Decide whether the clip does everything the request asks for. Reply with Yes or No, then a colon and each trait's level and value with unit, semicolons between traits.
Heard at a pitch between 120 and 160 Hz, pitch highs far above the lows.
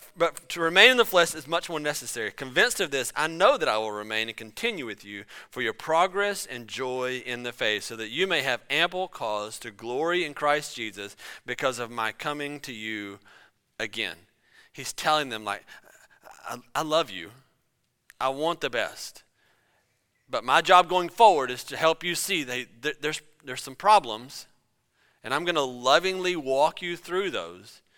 Yes: medium, 140 Hz; wide, 6.3 semitones